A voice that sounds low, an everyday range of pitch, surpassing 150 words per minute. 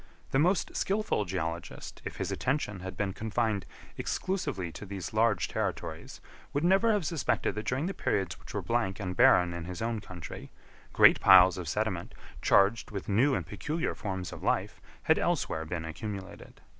No: low, 100 Hz; wide, 6.5 semitones; average, 170 wpm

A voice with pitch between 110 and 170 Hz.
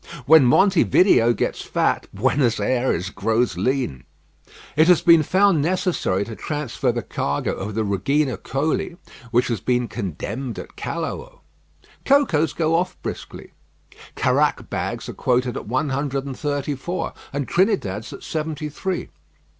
Yes: low, 135 Hz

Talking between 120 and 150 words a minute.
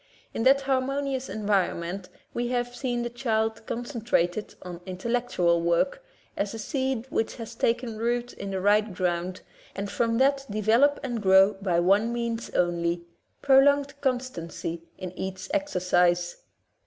Yes: average, 145 wpm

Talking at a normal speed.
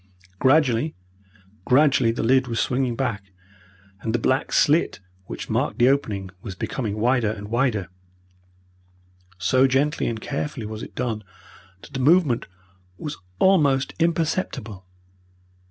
No: slow, 125 wpm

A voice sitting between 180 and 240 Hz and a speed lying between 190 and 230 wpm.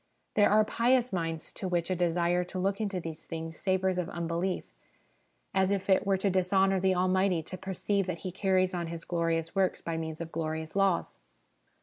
Yes: medium, 185 Hz; average, 195 wpm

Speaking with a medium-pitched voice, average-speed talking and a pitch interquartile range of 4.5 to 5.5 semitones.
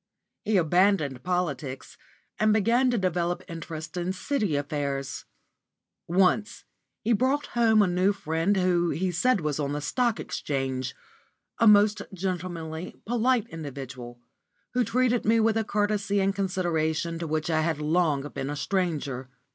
Yes: medium, 180 Hz; average, 145 wpm; average, 5.2 semitones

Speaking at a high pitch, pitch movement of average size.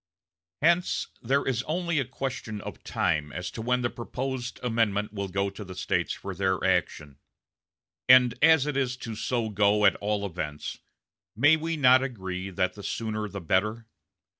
No: low, 110 Hz; average, 4.8 semitones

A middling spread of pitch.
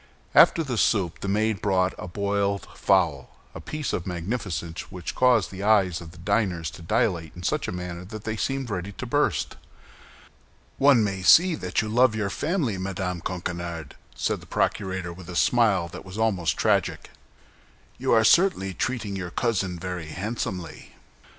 Yes: average, 3.8 semitones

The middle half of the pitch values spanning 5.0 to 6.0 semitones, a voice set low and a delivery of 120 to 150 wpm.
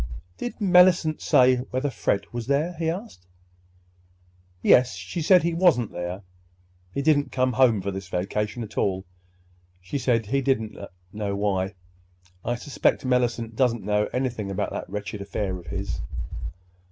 Yes: wide, 5.6 semitones; low, 120 Hz; average, 145 wpm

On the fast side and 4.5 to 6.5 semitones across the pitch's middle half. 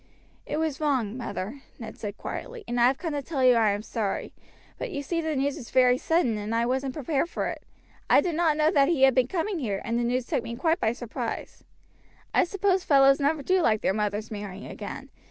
Yes: fast, 230 wpm; wide, 5.5 semitones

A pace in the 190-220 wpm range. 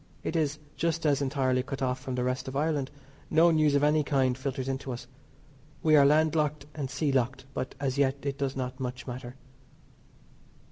Yes: average, 200 wpm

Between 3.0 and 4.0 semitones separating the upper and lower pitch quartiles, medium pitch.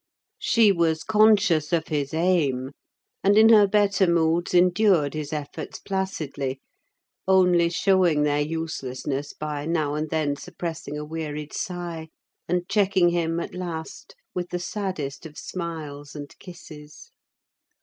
Yes: average, 3.6 semitones; medium, 165 Hz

